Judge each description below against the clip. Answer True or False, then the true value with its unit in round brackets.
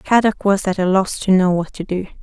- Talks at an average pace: False (270 wpm)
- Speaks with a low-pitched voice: False (190 Hz)